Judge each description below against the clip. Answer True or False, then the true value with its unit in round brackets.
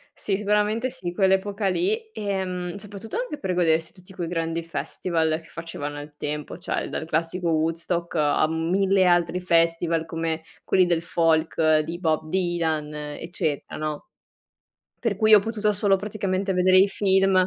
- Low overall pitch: False (175 Hz)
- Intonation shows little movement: False (3.1 semitones)